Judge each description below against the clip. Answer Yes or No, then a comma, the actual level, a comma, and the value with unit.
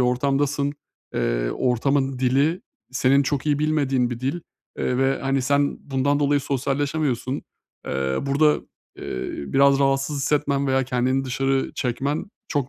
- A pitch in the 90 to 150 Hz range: Yes, low, 135 Hz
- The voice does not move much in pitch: Yes, narrow, 1.8 semitones